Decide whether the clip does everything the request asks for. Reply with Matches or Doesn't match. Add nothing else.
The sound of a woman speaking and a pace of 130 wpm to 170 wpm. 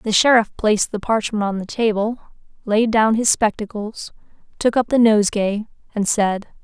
Matches